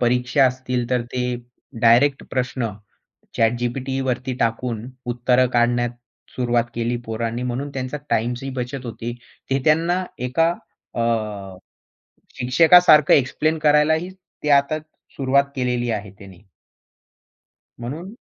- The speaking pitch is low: Yes, low, 125 Hz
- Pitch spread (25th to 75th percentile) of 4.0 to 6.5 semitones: No, average, 2.9 semitones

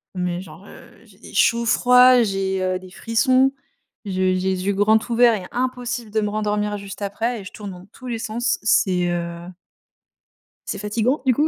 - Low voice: No, high, 210 Hz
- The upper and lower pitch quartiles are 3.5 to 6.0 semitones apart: Yes, average, 4.1 semitones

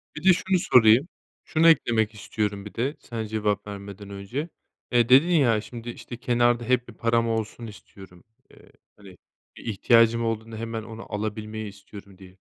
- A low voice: Yes, low, 115 Hz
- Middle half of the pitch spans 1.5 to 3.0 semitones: Yes, narrow, 2.6 semitones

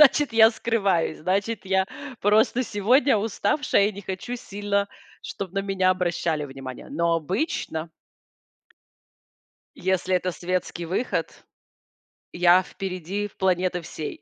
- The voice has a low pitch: No, high, 190 Hz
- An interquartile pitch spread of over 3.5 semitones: No, average, 2.9 semitones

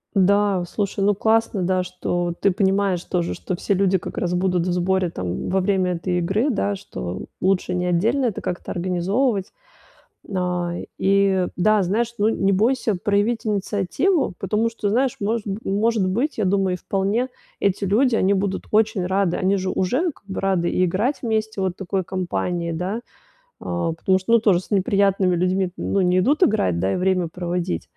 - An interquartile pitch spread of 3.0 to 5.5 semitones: No, narrow, 2.6 semitones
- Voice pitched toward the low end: No, high, 190 Hz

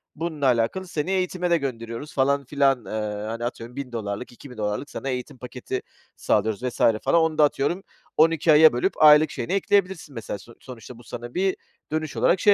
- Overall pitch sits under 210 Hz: Yes, low, 135 Hz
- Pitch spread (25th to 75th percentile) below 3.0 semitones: No, average, 5.1 semitones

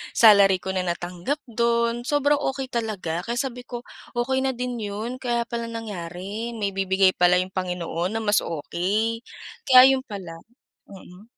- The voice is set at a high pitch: Yes, high, 220 Hz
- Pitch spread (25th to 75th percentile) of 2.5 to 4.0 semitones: No, average, 4.5 semitones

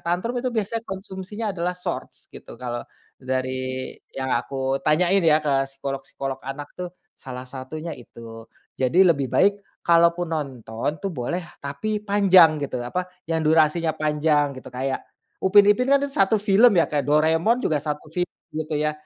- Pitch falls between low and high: Yes, medium, 155 Hz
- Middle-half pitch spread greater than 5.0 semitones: Yes, wide, 5.6 semitones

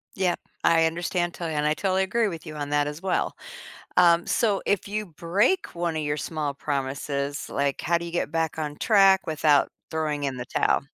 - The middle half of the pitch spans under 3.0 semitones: No, average, 3.5 semitones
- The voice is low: No, medium, 165 Hz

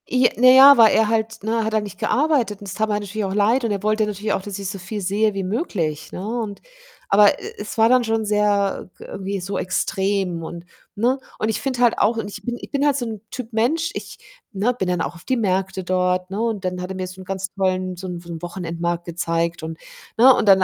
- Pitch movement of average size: Yes, average, 3.3 semitones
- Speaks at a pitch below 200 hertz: No, high, 205 Hz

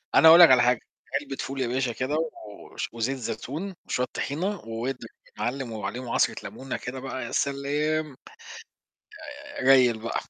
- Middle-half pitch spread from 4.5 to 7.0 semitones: No, average, 3.1 semitones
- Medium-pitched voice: No, low, 130 Hz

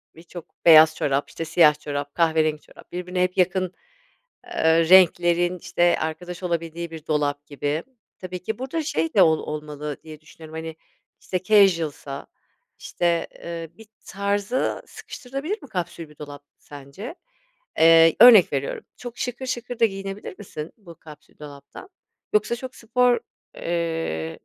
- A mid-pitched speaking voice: Yes, medium, 170 Hz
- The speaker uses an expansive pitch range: No, average, 4.0 semitones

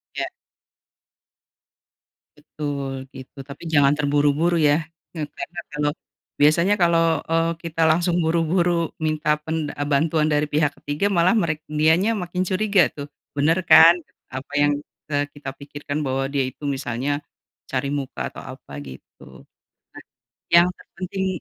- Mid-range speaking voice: Yes, medium, 150 Hz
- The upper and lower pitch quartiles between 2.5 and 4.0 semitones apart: Yes, average, 2.9 semitones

